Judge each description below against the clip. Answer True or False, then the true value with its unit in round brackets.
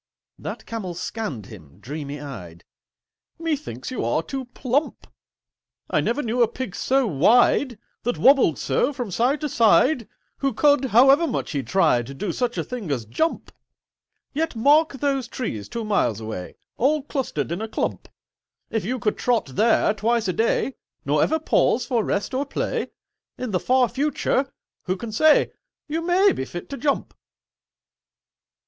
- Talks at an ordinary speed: True (160 wpm)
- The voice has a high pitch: True (235 Hz)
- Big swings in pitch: True (7.7 semitones)